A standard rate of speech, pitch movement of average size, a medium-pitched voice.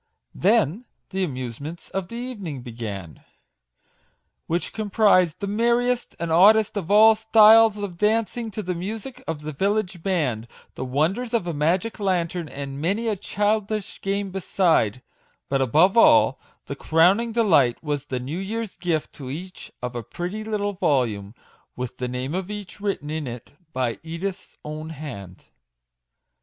No: average, 150 wpm; wide, 6.6 semitones; medium, 180 Hz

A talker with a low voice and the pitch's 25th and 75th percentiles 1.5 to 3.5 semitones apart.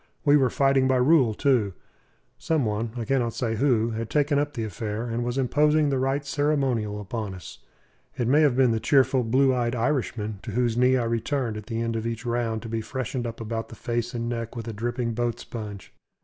Yes: low, 120 Hz; average, 2.9 semitones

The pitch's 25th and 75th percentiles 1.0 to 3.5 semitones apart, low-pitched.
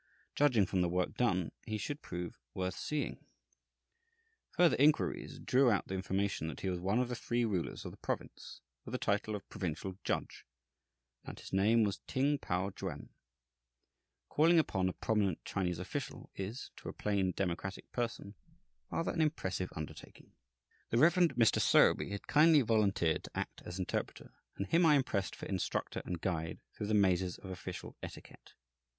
No: average, 5.1 semitones; low, 100 Hz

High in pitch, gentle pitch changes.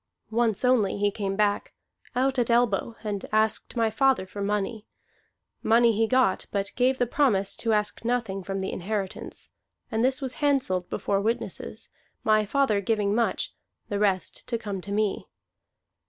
No: high, 215 Hz; average, 3.1 semitones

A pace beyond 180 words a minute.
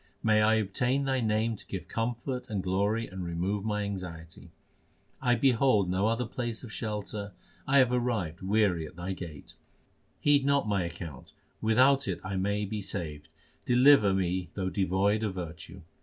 No: average, 165 wpm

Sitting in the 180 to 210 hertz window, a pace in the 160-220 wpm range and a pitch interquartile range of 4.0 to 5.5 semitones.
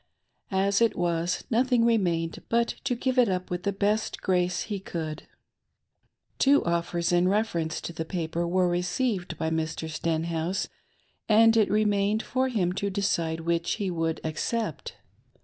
No: medium, 185 Hz; average, 150 wpm; average, 4.3 semitones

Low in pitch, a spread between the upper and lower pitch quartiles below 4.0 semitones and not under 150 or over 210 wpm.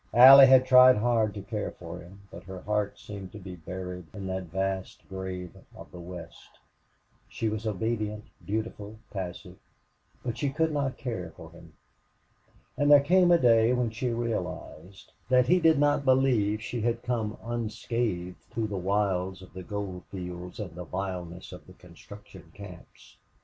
No: low, 105 Hz; average, 4.6 semitones; average, 165 wpm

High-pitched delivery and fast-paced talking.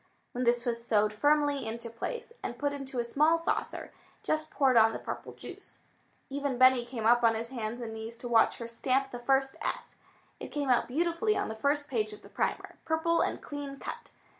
Yes: very high, 255 Hz; fast, 210 wpm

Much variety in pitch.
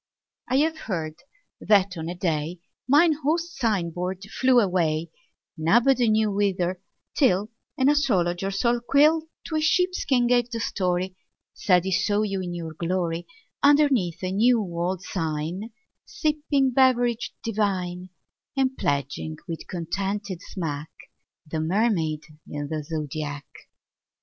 Yes: wide, 6.3 semitones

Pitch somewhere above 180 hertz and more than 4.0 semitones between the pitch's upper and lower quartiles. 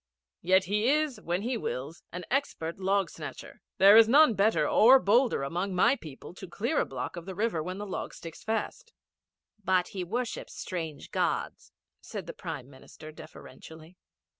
Yes: high, 190 Hz; average, 5.2 semitones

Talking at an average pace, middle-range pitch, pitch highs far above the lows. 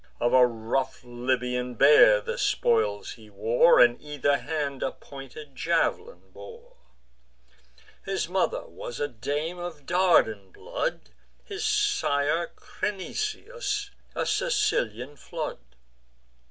No: slow, 110 wpm; medium, 145 Hz; wide, 8.2 semitones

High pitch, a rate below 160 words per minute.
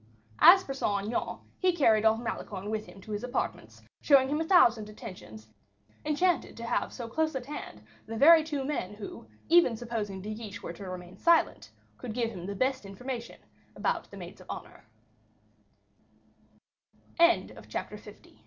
No: high, 230 Hz; average, 165 wpm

